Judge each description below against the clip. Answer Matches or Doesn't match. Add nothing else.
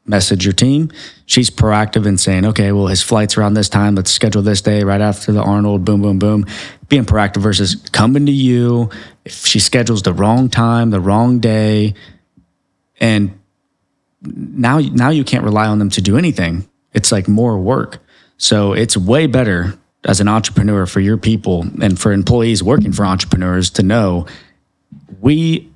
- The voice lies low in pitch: Matches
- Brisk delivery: Doesn't match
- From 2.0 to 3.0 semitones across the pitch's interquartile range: Matches